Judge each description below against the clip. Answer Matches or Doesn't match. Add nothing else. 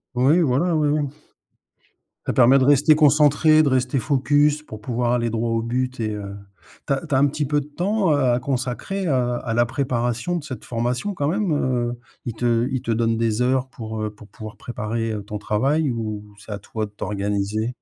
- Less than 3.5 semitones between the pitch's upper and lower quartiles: Doesn't match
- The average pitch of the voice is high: Doesn't match